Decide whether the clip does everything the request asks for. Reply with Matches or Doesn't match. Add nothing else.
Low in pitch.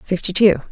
Doesn't match